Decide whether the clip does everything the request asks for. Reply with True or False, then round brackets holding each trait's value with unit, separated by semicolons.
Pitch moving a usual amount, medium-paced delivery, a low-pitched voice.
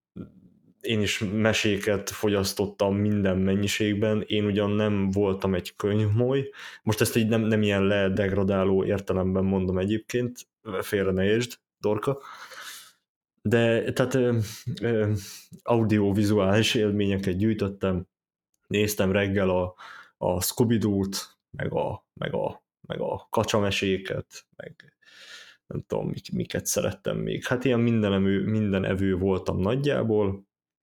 False (2.3 semitones; 120 wpm; 105 Hz)